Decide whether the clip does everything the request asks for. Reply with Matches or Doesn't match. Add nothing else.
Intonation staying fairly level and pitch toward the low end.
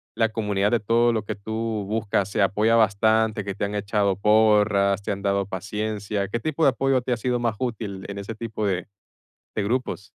Matches